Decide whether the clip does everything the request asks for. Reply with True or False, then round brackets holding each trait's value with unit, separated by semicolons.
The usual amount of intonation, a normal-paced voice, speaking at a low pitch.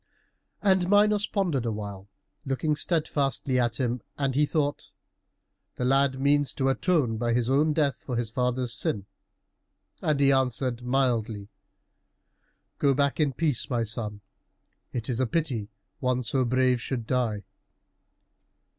True (3.3 semitones; 145 wpm; 130 Hz)